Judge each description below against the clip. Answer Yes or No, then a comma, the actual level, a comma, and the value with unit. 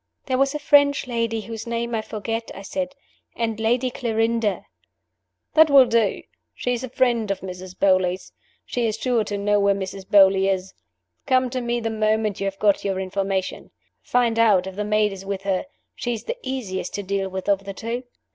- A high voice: Yes, high, 220 Hz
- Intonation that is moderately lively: Yes, average, 3.5 semitones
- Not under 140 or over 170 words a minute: No, fast, 205 wpm